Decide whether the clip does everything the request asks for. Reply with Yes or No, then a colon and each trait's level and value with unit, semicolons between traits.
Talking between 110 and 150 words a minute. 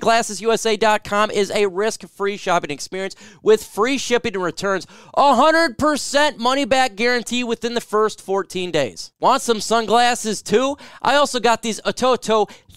Yes: slow, 135 wpm